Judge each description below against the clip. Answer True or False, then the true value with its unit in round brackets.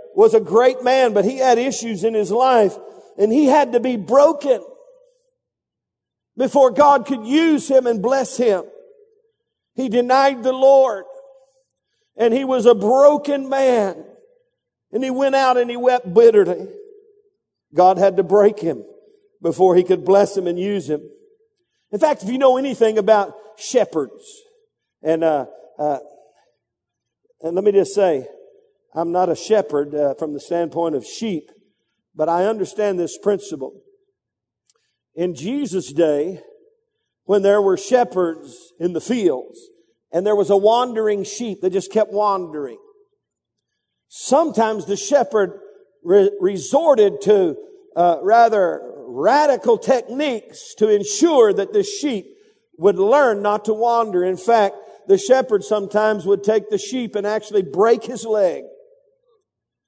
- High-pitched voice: True (245 Hz)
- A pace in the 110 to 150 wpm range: True (140 wpm)